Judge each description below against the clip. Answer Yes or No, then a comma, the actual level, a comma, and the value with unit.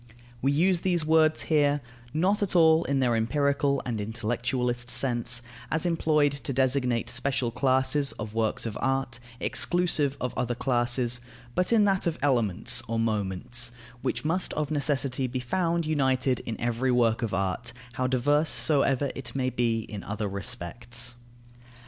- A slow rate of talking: No, average, 155 wpm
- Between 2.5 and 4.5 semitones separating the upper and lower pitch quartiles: Yes, average, 3.7 semitones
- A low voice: Yes, low, 130 Hz